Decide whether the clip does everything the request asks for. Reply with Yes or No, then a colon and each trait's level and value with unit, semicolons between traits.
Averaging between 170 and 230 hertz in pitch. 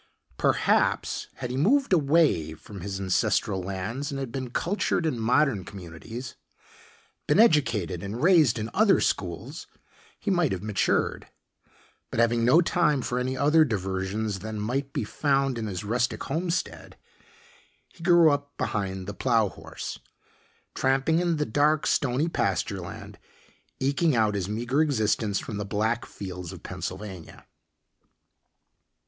No: low, 120 Hz